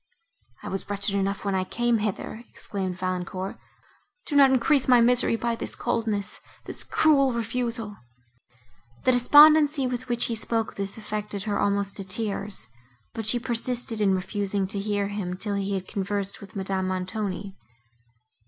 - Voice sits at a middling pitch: No, high, 210 Hz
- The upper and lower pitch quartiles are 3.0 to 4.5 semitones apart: Yes, average, 3.4 semitones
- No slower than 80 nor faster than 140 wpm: No, average, 155 wpm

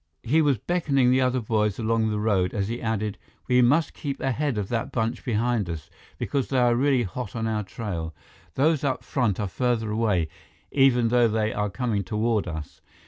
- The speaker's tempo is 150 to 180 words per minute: No, average, 195 wpm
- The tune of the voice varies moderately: Yes, average, 3.3 semitones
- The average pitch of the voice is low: Yes, low, 115 Hz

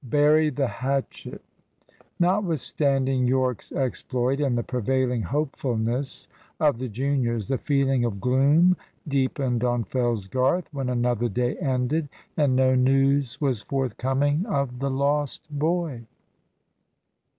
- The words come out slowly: Yes, slow, 115 wpm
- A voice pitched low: Yes, low, 130 Hz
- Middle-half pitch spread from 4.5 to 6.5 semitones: No, narrow, 2.4 semitones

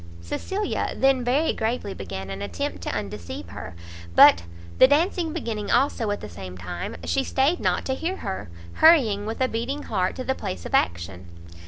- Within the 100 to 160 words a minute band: No, average, 180 wpm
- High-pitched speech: Yes, high, 210 Hz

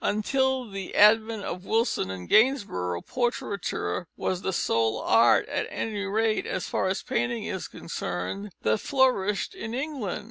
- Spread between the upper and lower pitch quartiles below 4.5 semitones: No, average, 4.8 semitones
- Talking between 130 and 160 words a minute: Yes, average, 145 wpm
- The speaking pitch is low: No, high, 210 Hz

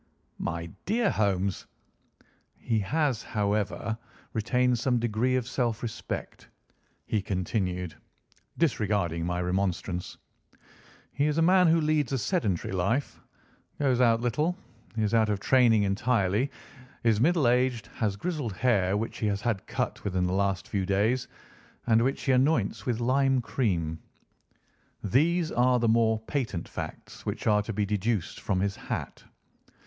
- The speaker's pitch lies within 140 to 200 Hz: No, low, 115 Hz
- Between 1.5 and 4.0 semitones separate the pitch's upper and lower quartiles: No, average, 4.5 semitones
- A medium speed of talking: Yes, average, 145 wpm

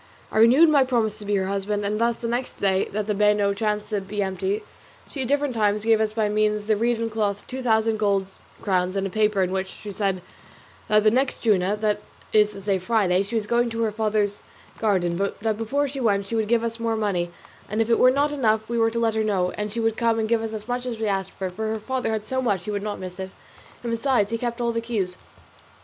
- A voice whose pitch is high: Yes, high, 215 Hz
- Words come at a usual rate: No, fast, 260 wpm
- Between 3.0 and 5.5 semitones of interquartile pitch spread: No, narrow, 2.4 semitones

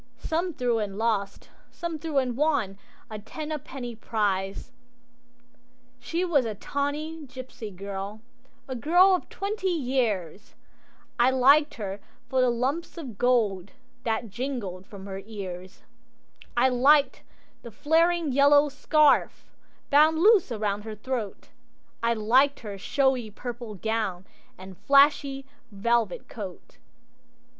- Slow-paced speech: Yes, slow, 125 wpm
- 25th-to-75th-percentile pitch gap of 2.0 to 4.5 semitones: No, wide, 5.5 semitones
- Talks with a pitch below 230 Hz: No, high, 245 Hz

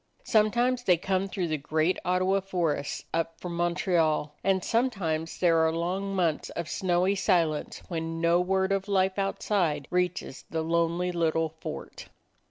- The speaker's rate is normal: Yes, average, 150 wpm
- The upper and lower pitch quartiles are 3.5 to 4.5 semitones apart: No, average, 2.8 semitones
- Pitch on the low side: No, medium, 175 Hz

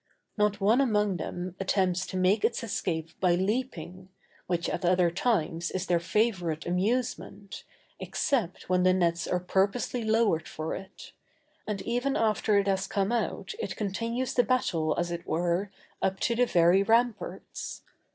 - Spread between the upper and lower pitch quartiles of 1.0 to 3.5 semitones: No, average, 4.0 semitones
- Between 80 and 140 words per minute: No, average, 155 wpm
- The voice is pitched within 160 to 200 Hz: Yes, high, 190 Hz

